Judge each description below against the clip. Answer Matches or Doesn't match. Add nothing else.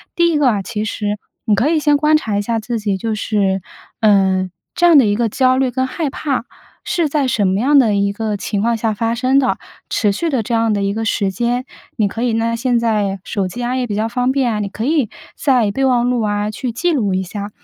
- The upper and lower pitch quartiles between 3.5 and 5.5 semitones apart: Matches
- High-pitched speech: Matches